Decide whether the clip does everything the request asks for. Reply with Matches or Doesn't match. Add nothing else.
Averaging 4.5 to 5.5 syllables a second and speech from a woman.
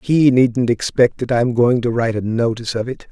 Doesn't match